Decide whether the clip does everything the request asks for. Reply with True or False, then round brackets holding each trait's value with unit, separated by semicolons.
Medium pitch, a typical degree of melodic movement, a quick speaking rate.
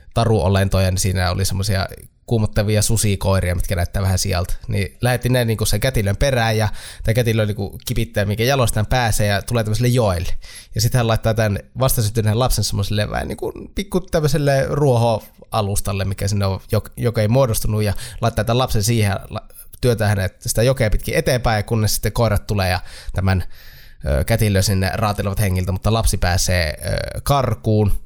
False (105 Hz; 3.0 semitones; 160 wpm)